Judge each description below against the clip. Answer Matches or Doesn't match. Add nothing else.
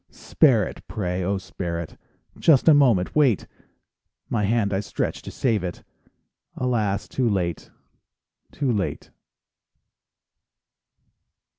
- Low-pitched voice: Matches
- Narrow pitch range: Doesn't match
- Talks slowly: Matches